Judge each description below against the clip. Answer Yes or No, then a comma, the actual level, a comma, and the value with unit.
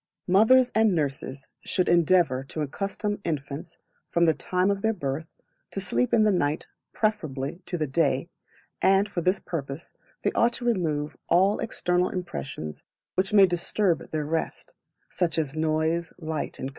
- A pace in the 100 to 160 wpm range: Yes, average, 155 wpm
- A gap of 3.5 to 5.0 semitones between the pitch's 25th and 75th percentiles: Yes, average, 4.5 semitones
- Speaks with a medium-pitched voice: Yes, medium, 170 Hz